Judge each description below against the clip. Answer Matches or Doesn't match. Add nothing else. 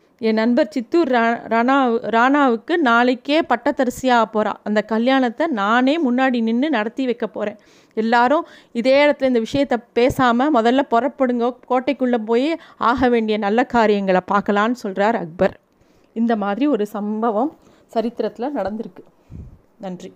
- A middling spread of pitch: Matches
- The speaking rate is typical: Matches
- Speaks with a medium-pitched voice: Doesn't match